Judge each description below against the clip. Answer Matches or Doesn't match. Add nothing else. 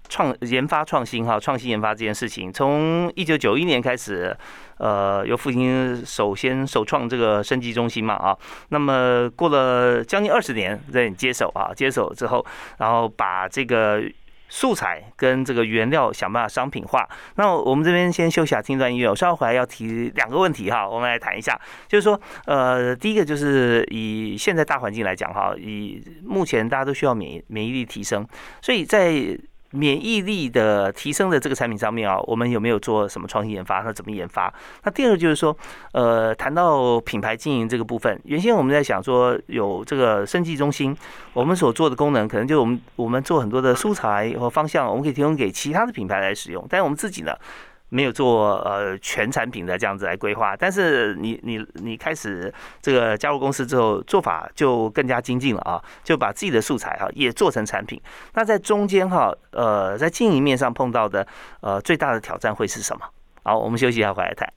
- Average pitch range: Matches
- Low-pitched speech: Matches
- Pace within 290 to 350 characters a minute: Matches